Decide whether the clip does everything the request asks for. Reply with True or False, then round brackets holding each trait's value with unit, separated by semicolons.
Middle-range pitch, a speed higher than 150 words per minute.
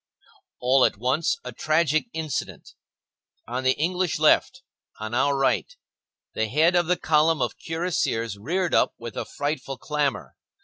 False (150 Hz; 145 wpm)